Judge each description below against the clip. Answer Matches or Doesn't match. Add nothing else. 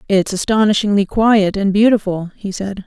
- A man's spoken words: Doesn't match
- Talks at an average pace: Matches